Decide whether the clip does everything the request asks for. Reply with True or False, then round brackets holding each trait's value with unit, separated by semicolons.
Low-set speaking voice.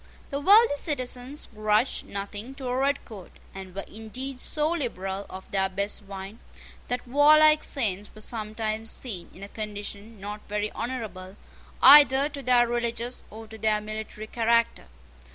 False (220 Hz)